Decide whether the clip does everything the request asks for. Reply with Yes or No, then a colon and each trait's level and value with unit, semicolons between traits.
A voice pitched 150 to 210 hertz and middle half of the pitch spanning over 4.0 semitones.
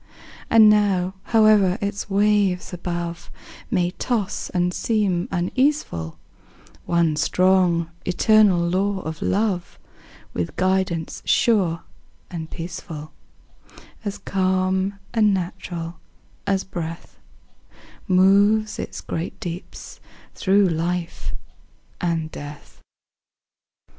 No: medium, 185 Hz; average, 2.9 semitones